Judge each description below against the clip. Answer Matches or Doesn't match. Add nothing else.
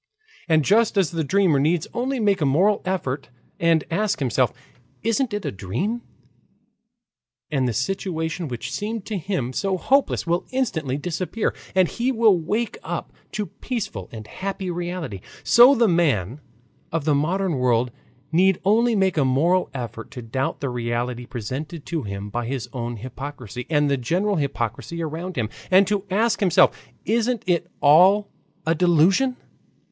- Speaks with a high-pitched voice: Doesn't match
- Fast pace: Doesn't match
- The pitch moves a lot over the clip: Matches